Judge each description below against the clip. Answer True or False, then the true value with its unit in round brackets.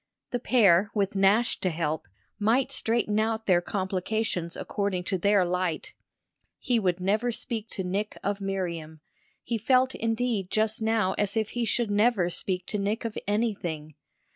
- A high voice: True (205 Hz)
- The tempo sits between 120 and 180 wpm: True (160 wpm)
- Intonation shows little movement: False (3.5 semitones)